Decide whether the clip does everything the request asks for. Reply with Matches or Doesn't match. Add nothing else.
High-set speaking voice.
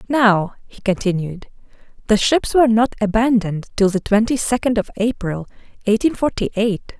Matches